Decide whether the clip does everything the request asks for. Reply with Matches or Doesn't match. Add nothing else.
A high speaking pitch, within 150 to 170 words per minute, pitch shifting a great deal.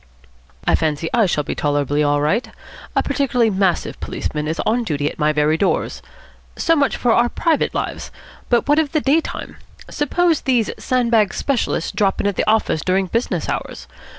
Doesn't match